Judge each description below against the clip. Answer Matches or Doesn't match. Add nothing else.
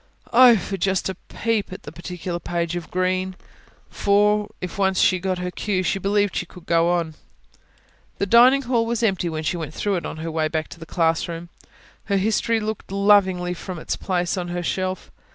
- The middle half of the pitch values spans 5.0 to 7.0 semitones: Doesn't match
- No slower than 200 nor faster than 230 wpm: Matches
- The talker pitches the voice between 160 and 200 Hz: Matches